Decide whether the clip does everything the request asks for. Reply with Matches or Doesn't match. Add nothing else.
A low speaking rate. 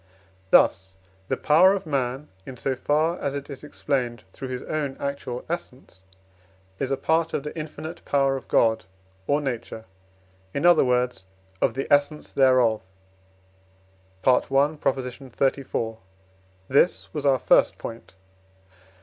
Matches